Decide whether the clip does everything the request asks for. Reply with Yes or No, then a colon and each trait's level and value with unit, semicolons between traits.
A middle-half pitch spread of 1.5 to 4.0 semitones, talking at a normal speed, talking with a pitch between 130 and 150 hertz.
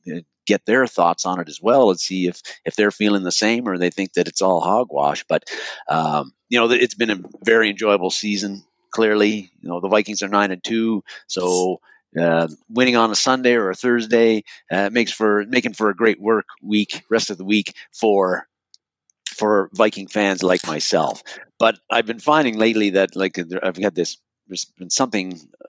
No: average, 3.3 semitones; average, 195 wpm; low, 105 Hz